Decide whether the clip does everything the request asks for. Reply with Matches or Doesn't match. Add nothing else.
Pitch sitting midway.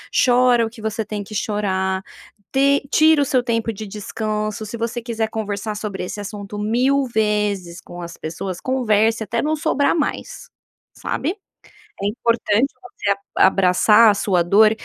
Doesn't match